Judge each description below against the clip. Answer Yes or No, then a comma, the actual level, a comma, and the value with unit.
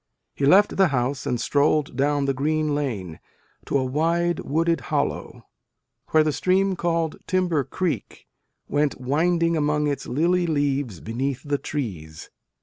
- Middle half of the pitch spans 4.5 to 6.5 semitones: No, average, 3.5 semitones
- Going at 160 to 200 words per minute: No, average, 145 wpm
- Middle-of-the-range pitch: Yes, medium, 145 Hz